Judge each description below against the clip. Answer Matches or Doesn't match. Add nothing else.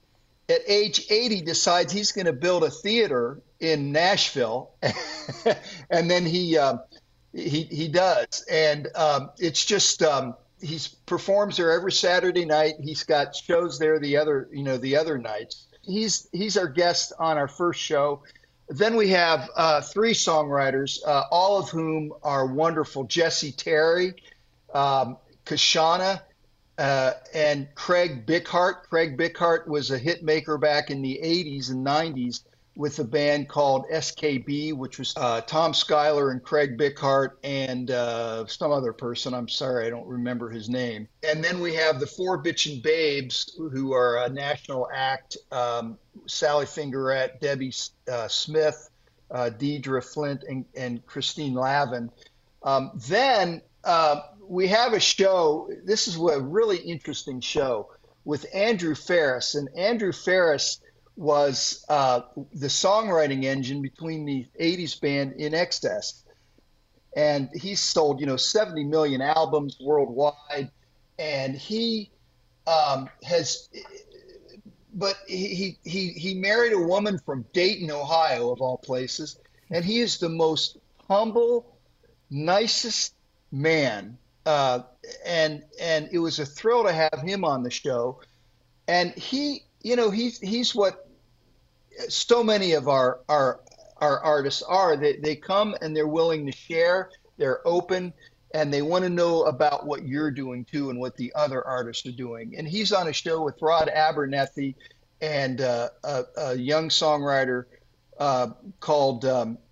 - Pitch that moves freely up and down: Doesn't match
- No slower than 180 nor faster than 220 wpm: Doesn't match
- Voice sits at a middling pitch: Matches